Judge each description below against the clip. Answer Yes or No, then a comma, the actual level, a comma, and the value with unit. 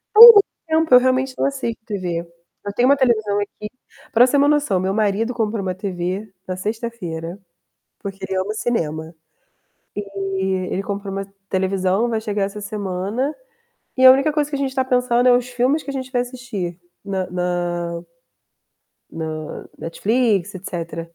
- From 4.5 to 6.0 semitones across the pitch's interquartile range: Yes, average, 5.1 semitones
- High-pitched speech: Yes, high, 205 Hz